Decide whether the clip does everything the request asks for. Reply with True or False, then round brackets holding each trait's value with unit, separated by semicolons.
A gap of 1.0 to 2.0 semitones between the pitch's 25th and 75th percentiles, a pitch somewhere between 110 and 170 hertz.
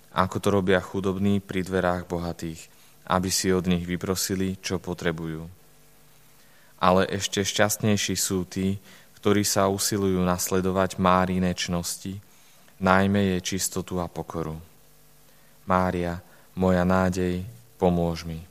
False (1.5 semitones; 95 Hz)